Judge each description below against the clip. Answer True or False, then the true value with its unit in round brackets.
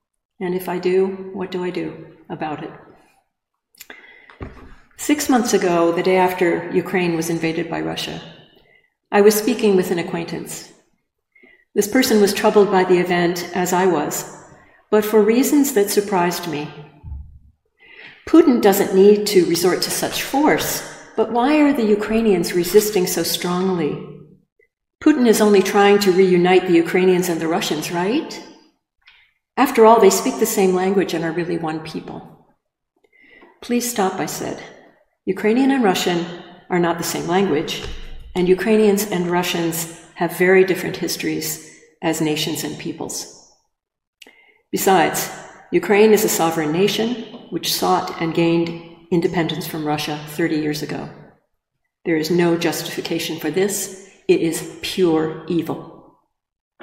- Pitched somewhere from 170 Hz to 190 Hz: True (185 Hz)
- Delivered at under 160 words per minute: True (140 wpm)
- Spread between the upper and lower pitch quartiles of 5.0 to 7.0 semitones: False (3.8 semitones)